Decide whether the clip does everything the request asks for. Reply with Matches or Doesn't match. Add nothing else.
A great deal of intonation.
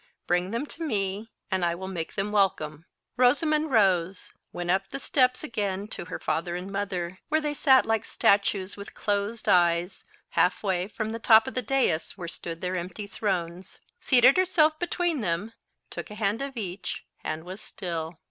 Doesn't match